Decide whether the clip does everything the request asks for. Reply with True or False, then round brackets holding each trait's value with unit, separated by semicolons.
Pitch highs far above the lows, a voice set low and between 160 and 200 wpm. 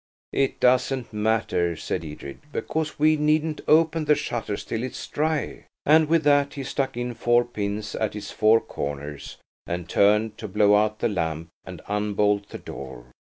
True (5.9 semitones; 110 Hz; 165 wpm)